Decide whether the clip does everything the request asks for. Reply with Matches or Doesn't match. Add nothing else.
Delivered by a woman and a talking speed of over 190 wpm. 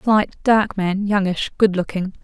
Doesn't match